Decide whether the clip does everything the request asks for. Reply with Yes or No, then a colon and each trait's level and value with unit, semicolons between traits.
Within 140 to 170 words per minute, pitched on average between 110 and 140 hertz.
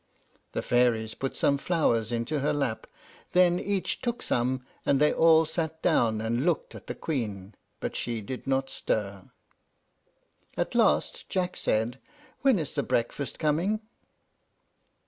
Yes: average, 145 wpm; low, 135 Hz